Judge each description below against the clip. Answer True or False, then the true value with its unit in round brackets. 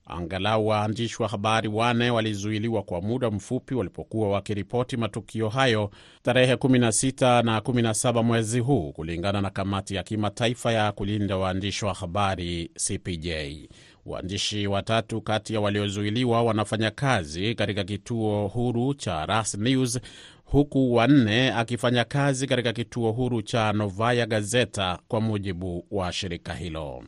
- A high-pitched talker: False (110 Hz)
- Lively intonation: False (3.2 semitones)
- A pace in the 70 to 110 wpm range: False (130 wpm)